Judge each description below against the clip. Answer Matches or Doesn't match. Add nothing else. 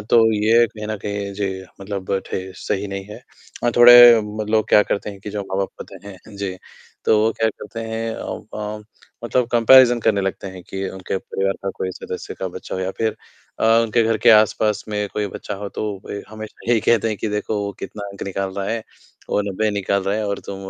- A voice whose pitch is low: Matches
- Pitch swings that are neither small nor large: Doesn't match